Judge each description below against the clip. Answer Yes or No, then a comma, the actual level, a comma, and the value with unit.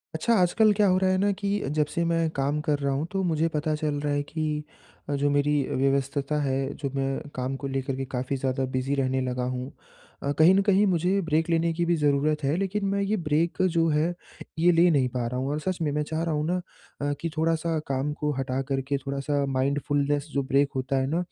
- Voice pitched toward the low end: No, medium, 150 Hz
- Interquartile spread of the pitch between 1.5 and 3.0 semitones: No, average, 3.5 semitones